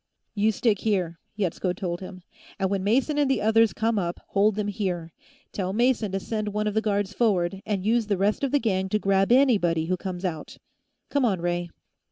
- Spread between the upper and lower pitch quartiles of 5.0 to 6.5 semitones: No, average, 3.1 semitones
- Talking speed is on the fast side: Yes, fast, 210 wpm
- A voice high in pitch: Yes, high, 200 Hz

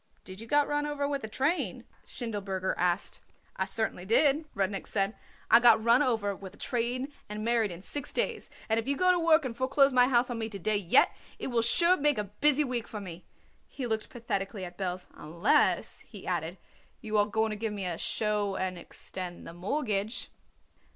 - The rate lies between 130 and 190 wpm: No, fast, 205 wpm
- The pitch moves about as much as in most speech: Yes, average, 4.9 semitones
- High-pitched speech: Yes, high, 220 Hz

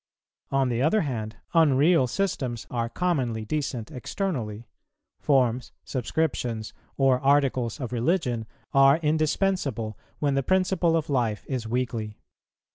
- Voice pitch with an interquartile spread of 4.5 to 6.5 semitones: Yes, average, 4.8 semitones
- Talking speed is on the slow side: Yes, slow, 120 wpm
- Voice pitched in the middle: No, low, 130 Hz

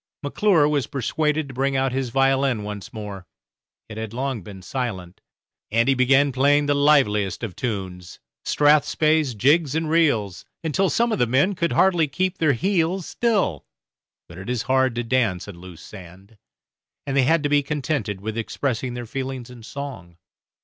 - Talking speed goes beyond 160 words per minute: Yes, average, 170 wpm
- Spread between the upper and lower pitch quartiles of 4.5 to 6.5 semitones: Yes, average, 5.2 semitones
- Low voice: Yes, low, 130 Hz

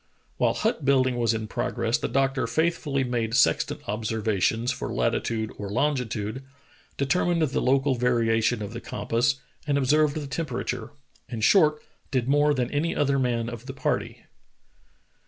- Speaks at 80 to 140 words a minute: No, average, 155 wpm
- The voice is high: No, low, 125 Hz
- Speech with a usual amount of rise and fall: Yes, average, 3.7 semitones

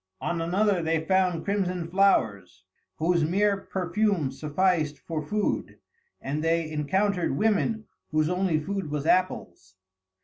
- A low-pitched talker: No, medium, 170 Hz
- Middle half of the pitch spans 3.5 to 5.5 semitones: Yes, average, 4.1 semitones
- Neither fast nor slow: No, slow, 125 wpm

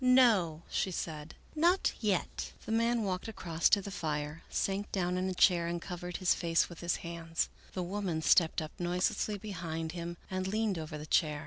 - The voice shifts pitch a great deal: No, average, 3.2 semitones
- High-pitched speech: No, medium, 175 Hz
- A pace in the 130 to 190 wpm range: No, average, 200 wpm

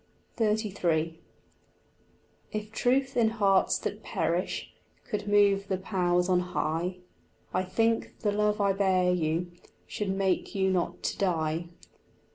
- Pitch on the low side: No, high, 190 Hz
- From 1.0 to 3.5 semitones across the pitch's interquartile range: Yes, average, 2.8 semitones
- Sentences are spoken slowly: Yes, slow, 125 wpm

